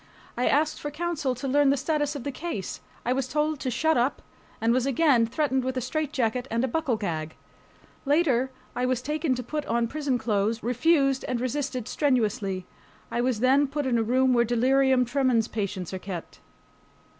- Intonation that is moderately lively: Yes, average, 3.5 semitones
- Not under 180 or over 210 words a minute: Yes, average, 190 wpm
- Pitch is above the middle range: Yes, very high, 255 Hz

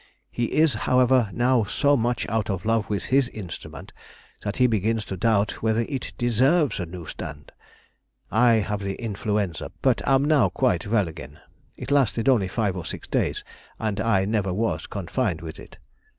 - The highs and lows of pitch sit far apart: No, average, 3.9 semitones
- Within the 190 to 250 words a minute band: No, average, 180 wpm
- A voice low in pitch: Yes, low, 110 Hz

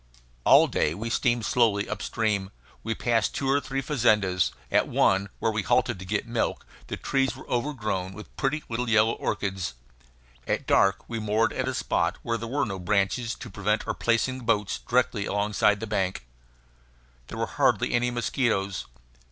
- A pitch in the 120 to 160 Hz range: No, low, 110 Hz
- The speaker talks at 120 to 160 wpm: No, average, 175 wpm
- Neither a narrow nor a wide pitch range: Yes, average, 3.3 semitones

